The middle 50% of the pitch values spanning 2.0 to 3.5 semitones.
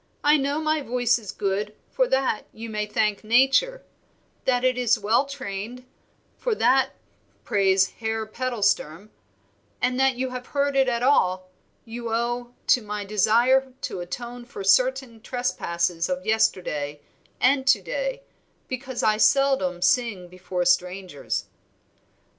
No: average, 4.6 semitones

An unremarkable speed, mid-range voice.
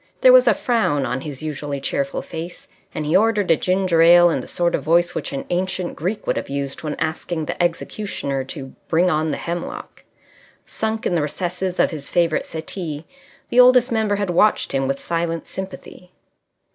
Yes: average, 190 wpm; medium, 170 Hz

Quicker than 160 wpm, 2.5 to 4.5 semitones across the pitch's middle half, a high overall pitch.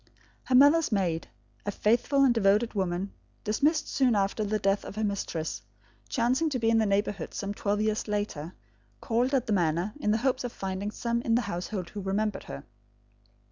Yes: average, 185 wpm; average, 3.4 semitones; high, 210 Hz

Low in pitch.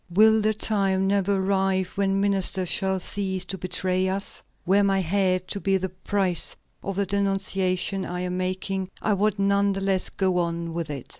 No: high, 190 Hz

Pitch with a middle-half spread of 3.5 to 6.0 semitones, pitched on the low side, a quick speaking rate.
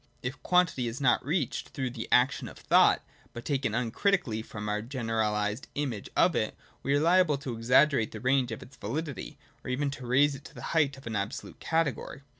Yes: average, 4.1 semitones; low, 130 Hz; fast, 210 wpm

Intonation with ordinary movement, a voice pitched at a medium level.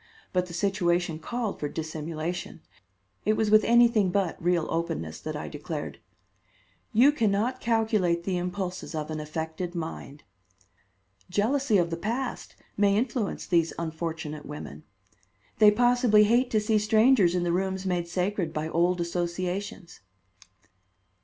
Yes: average, 4.1 semitones; medium, 180 Hz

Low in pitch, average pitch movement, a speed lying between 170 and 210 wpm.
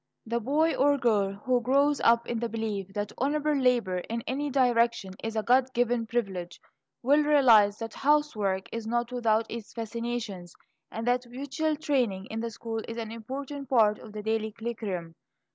No: high, 235 Hz; average, 3.3 semitones; average, 175 wpm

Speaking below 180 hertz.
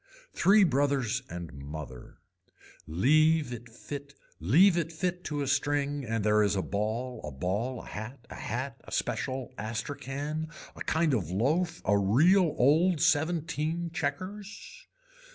Yes: medium, 140 Hz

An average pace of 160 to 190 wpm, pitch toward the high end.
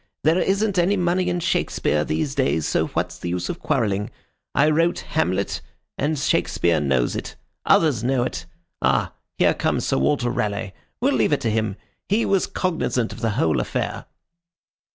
No: average, 170 wpm; low, 120 Hz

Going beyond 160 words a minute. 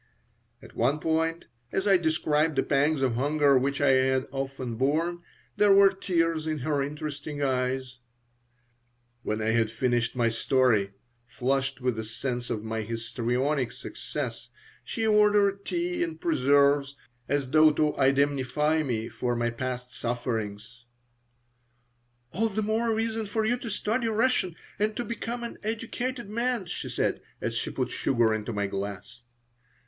No: average, 150 wpm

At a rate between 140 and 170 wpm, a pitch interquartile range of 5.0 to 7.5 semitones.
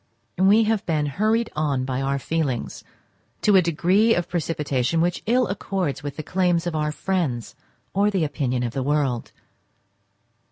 Yes: average, 160 wpm; wide, 5.5 semitones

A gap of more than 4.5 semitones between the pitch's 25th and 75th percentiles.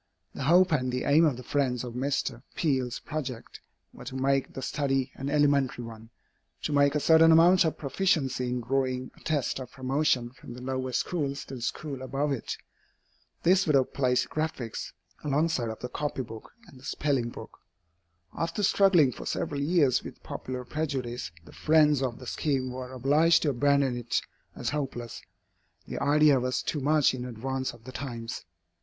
No: average, 2.9 semitones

